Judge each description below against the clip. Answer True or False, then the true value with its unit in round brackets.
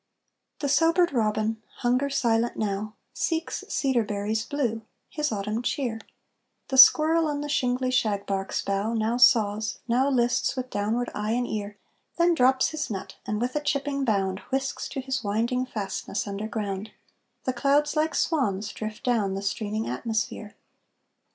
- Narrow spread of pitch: False (4.2 semitones)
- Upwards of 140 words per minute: True (150 wpm)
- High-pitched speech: True (235 Hz)